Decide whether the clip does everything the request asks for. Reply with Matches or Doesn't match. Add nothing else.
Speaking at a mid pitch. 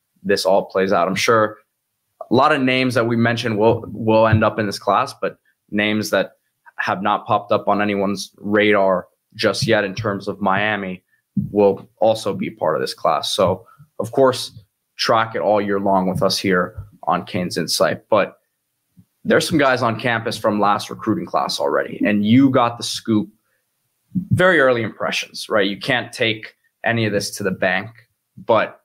Doesn't match